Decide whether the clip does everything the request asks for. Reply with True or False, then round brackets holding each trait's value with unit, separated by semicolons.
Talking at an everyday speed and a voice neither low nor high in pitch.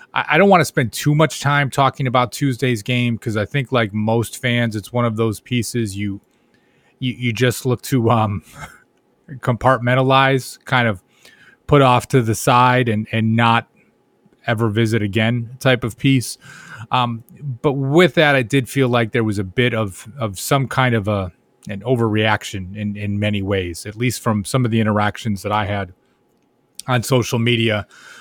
False (180 wpm; 120 Hz)